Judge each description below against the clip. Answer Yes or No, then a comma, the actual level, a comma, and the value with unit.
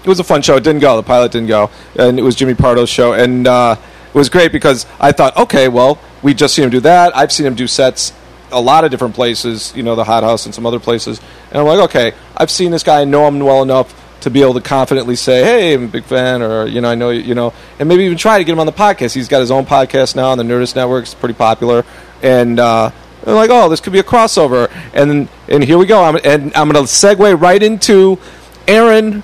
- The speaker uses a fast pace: Yes, fast, 265 wpm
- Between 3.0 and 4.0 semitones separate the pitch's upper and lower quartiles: No, average, 4.7 semitones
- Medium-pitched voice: No, low, 130 Hz